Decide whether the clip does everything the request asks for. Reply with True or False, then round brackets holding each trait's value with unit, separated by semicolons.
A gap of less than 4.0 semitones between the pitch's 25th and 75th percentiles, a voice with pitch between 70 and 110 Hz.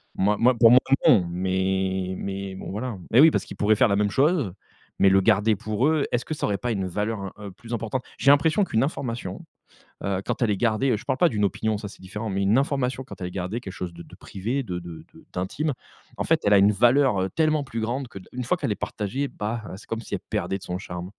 False (4.5 semitones; 105 Hz)